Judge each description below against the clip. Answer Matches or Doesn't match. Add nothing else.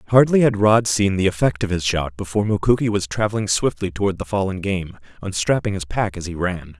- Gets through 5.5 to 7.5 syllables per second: Matches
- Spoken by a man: Matches